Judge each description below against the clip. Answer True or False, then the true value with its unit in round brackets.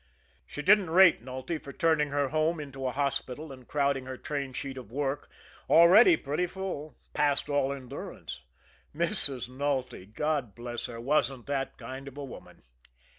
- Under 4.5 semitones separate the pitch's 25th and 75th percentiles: True (2.8 semitones)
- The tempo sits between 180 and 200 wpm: False (160 wpm)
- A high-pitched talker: False (140 Hz)